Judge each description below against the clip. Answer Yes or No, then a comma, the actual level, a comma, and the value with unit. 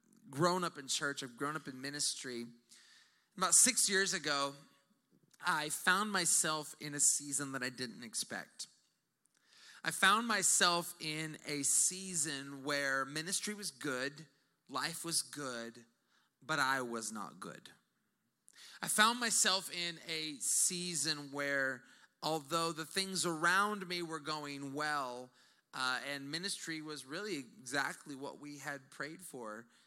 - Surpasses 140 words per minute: No, slow, 135 wpm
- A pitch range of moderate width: Yes, average, 4.1 semitones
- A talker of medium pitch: Yes, medium, 150 Hz